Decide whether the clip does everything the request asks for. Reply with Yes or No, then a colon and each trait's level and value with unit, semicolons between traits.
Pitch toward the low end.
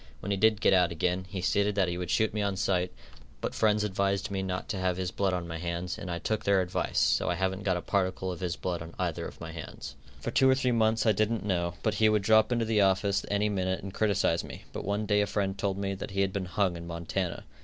Yes: very low, 95 Hz